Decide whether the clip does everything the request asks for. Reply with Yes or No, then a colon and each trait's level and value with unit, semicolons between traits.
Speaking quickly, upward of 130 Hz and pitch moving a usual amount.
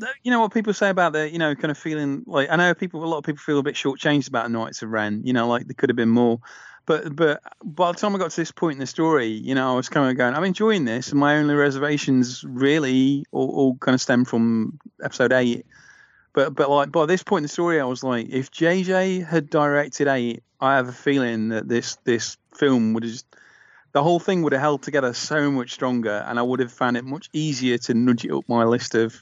Yes: fast, 260 wpm; medium, 140 Hz; average, 4.2 semitones